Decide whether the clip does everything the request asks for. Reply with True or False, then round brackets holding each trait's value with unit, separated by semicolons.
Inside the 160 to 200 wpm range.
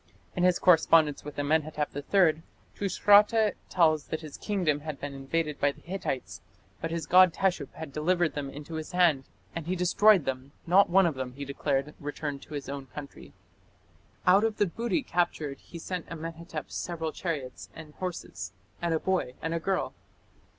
True (175 wpm)